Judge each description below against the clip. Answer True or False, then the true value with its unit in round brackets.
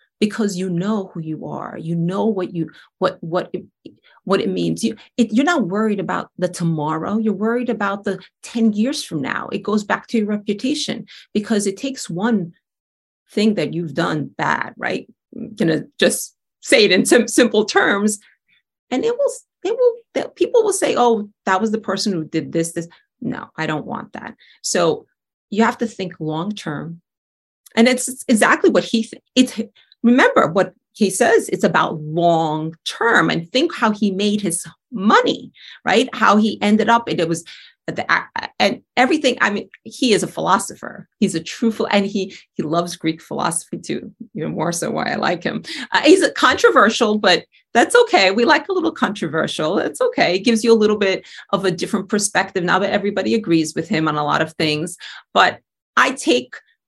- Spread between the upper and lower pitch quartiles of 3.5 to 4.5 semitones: False (5.5 semitones)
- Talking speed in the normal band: True (190 wpm)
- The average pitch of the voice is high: True (210 Hz)